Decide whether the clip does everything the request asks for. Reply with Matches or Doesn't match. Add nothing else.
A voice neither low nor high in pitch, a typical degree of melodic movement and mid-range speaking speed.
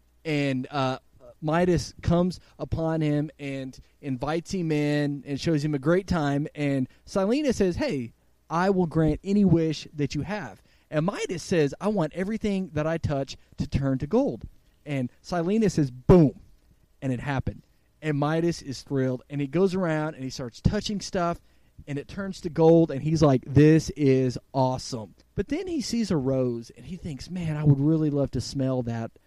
Matches